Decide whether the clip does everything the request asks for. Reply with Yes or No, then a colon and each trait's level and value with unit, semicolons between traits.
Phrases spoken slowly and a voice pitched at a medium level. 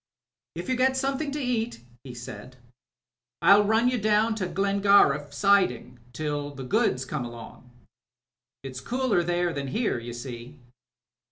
No: average, 145 wpm; medium, 175 Hz